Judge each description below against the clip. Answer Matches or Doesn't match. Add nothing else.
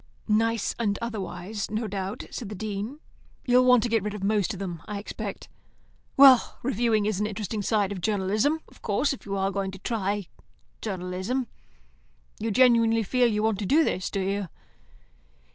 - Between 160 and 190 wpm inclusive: Matches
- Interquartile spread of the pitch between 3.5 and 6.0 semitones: Doesn't match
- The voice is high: Matches